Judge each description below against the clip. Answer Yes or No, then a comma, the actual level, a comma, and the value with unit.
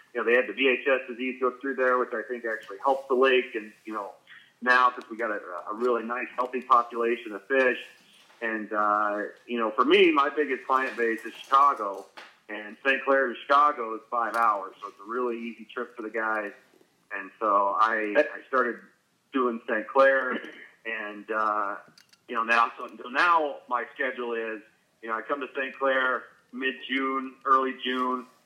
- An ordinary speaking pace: Yes, average, 190 wpm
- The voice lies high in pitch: No, low, 125 Hz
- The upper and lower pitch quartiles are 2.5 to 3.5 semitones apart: Yes, average, 3.0 semitones